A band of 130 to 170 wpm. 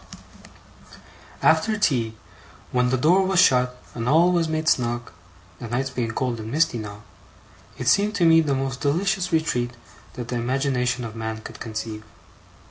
Yes: average, 160 wpm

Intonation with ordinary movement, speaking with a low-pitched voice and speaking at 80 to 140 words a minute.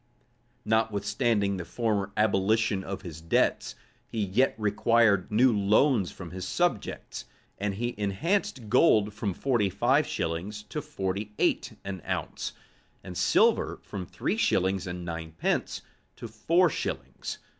Yes: average, 3.5 semitones; low, 105 Hz; slow, 135 wpm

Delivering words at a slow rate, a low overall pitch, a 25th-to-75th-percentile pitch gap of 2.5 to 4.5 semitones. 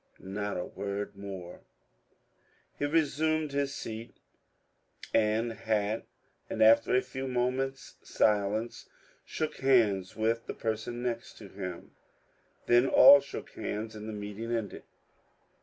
Yes: slow, 120 wpm; low, 115 Hz; average, 3.8 semitones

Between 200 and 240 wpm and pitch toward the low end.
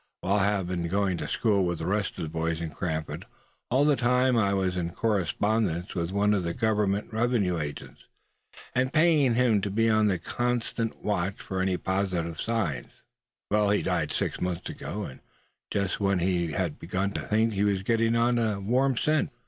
No: average, 190 wpm; low, 100 Hz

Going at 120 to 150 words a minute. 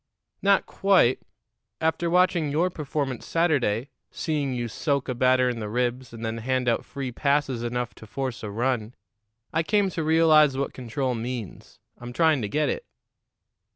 No: average, 165 wpm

